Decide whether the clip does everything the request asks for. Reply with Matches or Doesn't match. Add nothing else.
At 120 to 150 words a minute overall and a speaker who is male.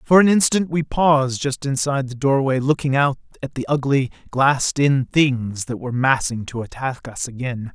Doesn't match